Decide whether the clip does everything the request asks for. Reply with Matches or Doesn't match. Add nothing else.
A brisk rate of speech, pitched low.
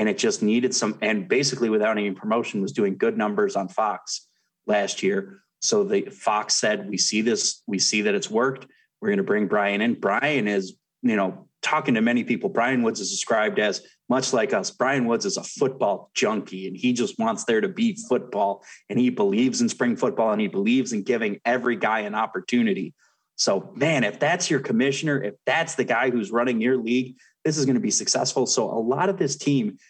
Matches